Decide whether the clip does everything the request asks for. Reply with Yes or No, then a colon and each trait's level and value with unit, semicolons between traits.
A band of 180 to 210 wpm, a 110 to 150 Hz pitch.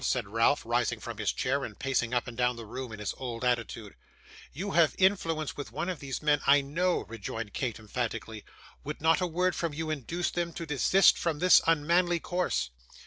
Yes: average, 200 wpm; medium, 140 Hz